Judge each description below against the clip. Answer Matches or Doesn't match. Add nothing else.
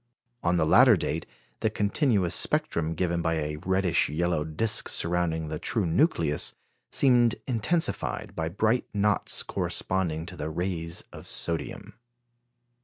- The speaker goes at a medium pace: Doesn't match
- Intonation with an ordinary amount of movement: Matches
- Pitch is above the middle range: Doesn't match